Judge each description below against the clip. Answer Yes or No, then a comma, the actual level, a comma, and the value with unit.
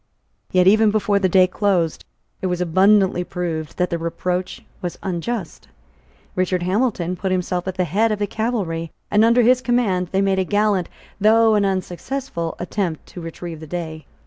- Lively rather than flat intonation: No, average, 3.1 semitones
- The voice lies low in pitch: No, medium, 185 Hz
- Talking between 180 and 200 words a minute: No, average, 170 wpm